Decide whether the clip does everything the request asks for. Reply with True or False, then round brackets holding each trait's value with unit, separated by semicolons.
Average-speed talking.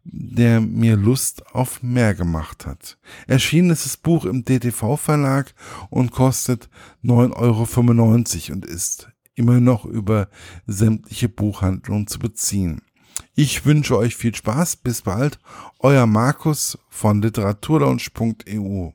False (115 wpm)